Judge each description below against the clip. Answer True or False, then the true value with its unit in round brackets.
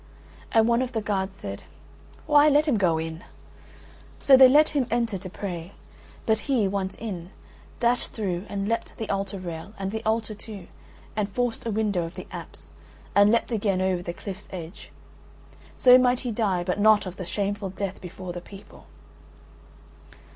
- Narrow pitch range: False (3.6 semitones)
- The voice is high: True (205 Hz)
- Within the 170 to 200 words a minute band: True (175 wpm)